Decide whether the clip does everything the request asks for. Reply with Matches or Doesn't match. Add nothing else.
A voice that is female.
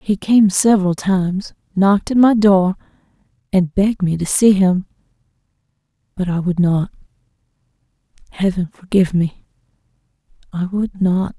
Matches